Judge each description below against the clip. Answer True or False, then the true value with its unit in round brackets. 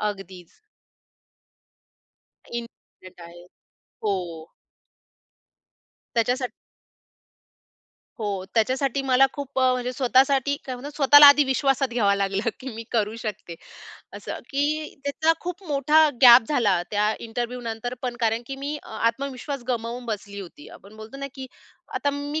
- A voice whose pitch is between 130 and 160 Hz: False (245 Hz)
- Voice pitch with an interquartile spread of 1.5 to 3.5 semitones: False (4.2 semitones)